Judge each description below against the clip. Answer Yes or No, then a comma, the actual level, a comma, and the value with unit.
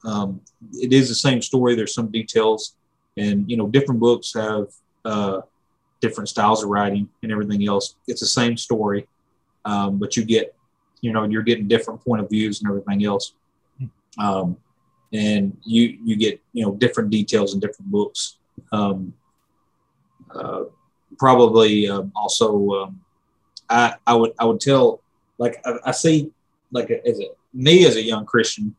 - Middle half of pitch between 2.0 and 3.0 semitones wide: No, average, 3.6 semitones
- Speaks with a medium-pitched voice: No, low, 110 Hz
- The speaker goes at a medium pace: Yes, average, 165 wpm